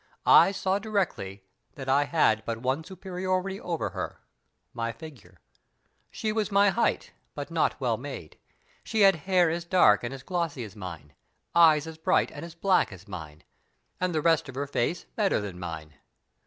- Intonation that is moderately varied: No, wide, 8.6 semitones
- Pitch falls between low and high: Yes, medium, 160 Hz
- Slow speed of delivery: No, average, 175 wpm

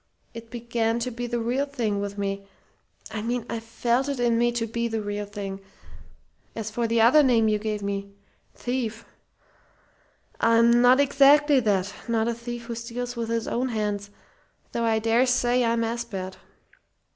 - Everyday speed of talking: Yes, average, 175 wpm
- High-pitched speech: Yes, high, 230 Hz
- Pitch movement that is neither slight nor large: No, narrow, 2.0 semitones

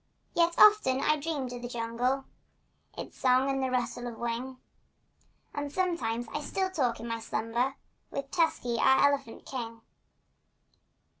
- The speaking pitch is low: No, very high, 260 Hz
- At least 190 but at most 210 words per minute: No, average, 140 wpm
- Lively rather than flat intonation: No, average, 3.2 semitones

